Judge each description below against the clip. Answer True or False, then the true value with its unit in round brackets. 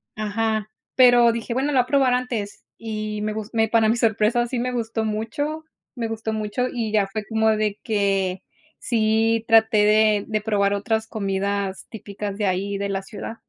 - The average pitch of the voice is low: False (220 Hz)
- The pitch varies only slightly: True (1.9 semitones)